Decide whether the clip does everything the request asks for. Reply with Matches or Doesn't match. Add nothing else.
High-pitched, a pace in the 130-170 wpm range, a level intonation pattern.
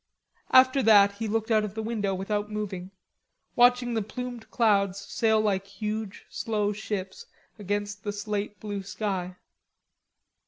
Matches